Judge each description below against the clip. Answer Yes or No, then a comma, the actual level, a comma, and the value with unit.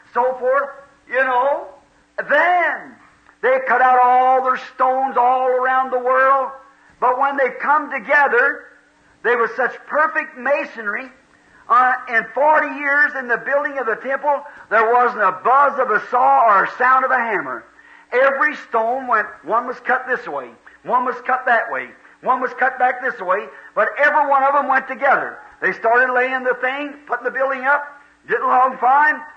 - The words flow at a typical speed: Yes, average, 175 wpm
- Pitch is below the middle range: No, very high, 265 Hz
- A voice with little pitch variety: Yes, narrow, 2.3 semitones